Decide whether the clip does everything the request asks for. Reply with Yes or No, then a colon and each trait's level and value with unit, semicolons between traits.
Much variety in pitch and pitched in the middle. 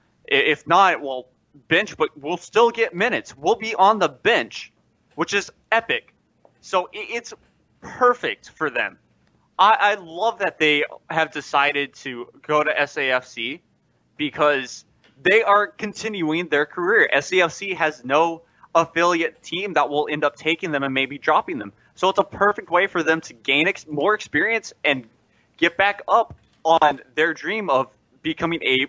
Yes: wide, 5.8 semitones; medium, 160 Hz